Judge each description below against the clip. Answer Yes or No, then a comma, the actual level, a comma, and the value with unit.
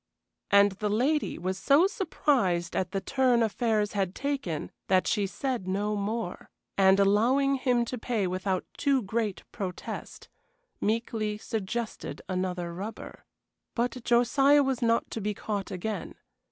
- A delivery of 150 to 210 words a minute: No, average, 140 wpm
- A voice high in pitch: Yes, high, 215 Hz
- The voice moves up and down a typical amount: Yes, average, 4.3 semitones